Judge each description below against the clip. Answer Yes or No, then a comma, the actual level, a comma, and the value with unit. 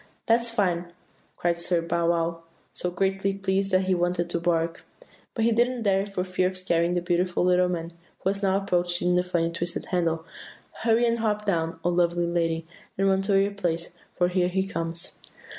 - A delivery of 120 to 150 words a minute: No, average, 190 wpm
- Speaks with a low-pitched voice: No, medium, 180 Hz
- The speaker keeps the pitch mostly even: Yes, narrow, 2.3 semitones